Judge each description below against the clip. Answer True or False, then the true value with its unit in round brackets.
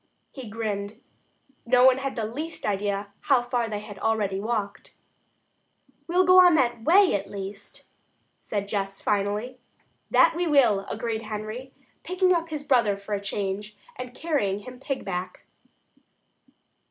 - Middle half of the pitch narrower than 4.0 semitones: False (4.8 semitones)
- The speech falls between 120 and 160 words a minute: True (140 wpm)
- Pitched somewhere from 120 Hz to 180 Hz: False (225 Hz)